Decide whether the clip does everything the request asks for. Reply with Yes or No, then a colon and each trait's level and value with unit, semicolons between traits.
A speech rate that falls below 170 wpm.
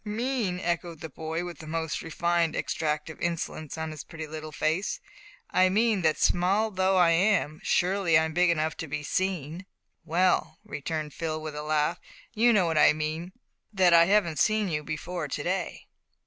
No: average, 180 wpm